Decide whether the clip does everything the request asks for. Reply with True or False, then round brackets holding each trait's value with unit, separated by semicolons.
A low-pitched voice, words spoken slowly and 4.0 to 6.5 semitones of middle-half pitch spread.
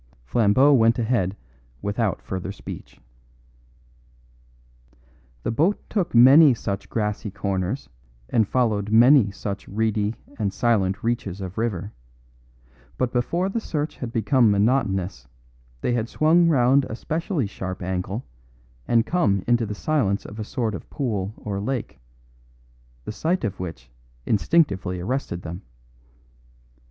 True (110 Hz; 125 wpm; 4.6 semitones)